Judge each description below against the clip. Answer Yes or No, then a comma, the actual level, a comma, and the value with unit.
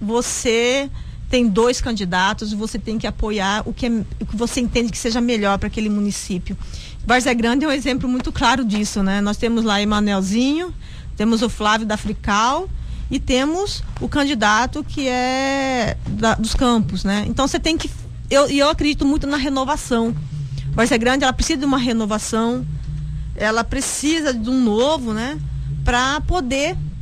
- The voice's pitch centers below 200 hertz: No, high, 235 Hz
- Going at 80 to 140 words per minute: No, average, 165 wpm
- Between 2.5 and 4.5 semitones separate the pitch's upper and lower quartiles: Yes, average, 4.0 semitones